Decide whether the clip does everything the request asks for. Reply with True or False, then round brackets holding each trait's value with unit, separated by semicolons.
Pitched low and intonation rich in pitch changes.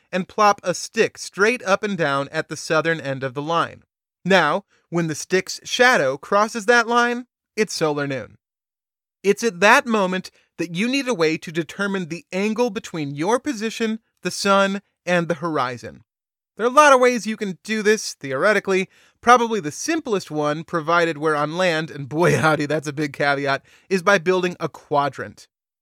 False (185 Hz; 5.7 semitones)